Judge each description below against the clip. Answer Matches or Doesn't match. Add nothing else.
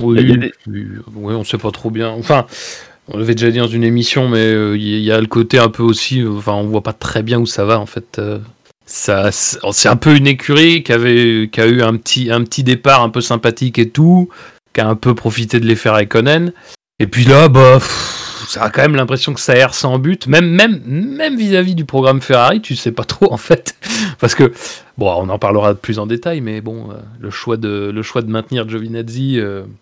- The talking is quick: Matches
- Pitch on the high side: Doesn't match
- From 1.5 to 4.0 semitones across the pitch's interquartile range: Matches